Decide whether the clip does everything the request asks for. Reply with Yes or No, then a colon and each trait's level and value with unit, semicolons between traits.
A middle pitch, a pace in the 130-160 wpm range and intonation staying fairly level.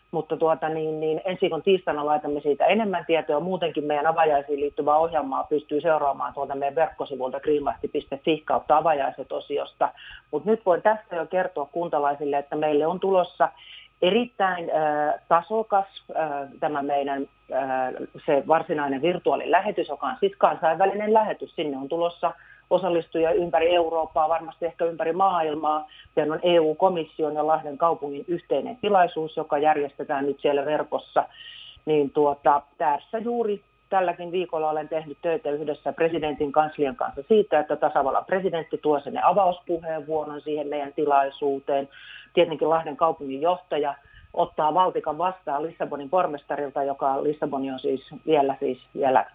No: medium, 155 Hz; average, 135 wpm; average, 3.0 semitones